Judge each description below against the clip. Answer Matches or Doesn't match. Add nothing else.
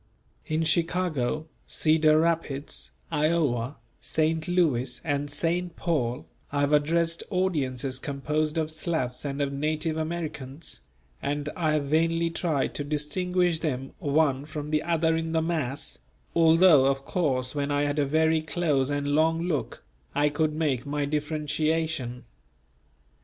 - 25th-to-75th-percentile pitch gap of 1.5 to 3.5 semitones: Matches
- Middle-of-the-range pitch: Matches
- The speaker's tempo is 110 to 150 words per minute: Matches